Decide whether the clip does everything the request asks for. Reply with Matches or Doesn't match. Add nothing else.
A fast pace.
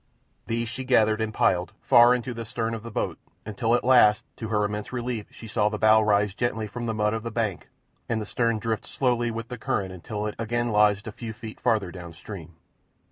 Matches